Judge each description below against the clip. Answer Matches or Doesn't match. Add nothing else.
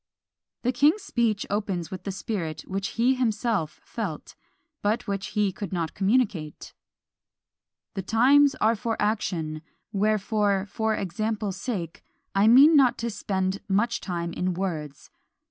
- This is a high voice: Matches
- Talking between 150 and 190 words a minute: Doesn't match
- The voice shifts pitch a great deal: Doesn't match